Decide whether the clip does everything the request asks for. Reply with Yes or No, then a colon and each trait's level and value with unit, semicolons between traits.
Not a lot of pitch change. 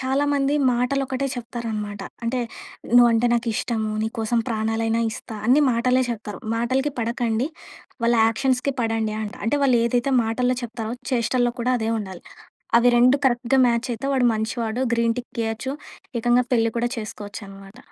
Yes: narrow, 2.1 semitones